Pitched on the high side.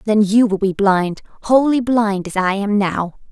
Yes: high, 210 Hz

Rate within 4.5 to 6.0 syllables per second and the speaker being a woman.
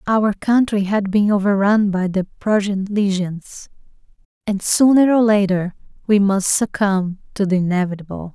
Yes: 4.6 syllables/s; female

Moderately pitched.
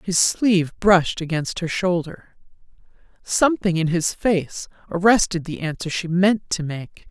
Yes: medium, 180 Hz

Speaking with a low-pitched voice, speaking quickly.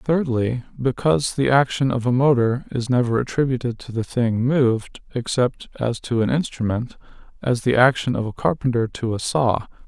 No: low, 125 Hz; average, 170 wpm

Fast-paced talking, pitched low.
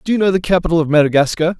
No: fast, 265 wpm; medium, 170 Hz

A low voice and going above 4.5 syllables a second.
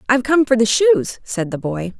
No: high, 245 Hz; 5.1 syllables/s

